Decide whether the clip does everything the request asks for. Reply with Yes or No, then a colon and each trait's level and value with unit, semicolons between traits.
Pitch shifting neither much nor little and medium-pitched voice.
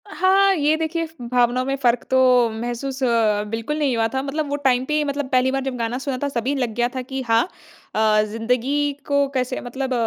No: average, 3.0 semitones; very high, 260 Hz